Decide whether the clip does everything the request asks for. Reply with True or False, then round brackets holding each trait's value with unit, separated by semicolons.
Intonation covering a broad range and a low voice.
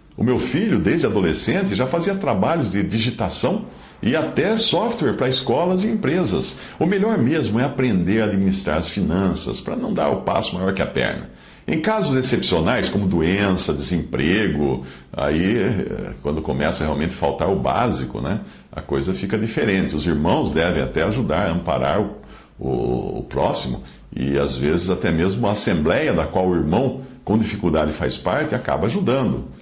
True (8.8 semitones; 95 Hz)